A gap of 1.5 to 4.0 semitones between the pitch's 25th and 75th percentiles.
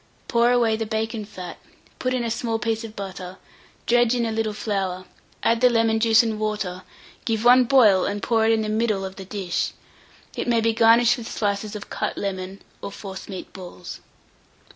Yes: average, 2.7 semitones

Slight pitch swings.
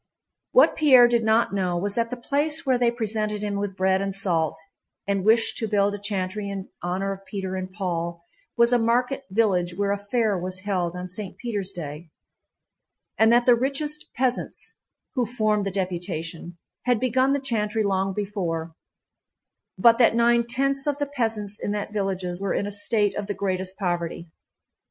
No: average, 4.0 semitones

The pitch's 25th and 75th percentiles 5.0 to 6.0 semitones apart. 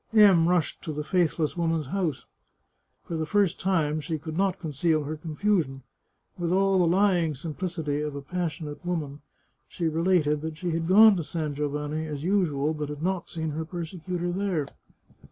No: average, 3.0 semitones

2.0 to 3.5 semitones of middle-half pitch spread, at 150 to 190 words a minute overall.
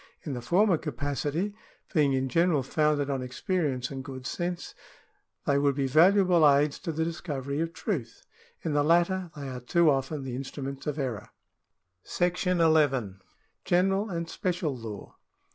No: average, 4.2 semitones; average, 170 wpm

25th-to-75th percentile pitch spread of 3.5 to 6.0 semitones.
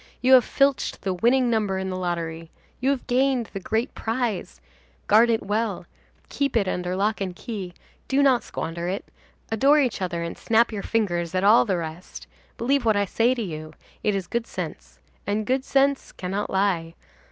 Yes: average, 4.9 semitones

